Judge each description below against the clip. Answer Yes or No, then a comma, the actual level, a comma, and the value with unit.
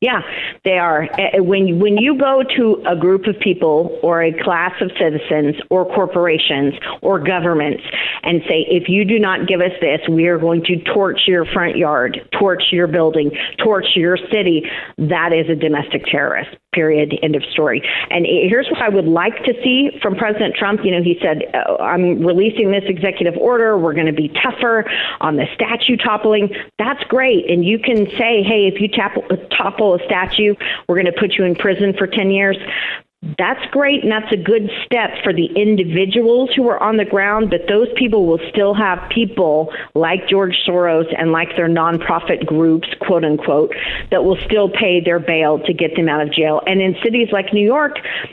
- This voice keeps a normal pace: Yes, average, 195 wpm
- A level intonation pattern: No, average, 4.1 semitones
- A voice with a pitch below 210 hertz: Yes, high, 190 Hz